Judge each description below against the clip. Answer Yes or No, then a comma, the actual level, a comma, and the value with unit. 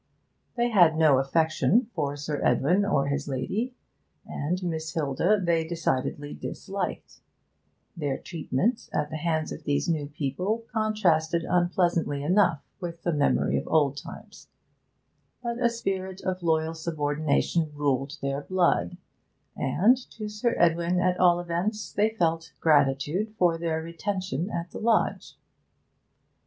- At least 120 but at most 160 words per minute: Yes, slow, 135 wpm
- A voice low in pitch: No, medium, 170 Hz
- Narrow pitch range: No, average, 4.3 semitones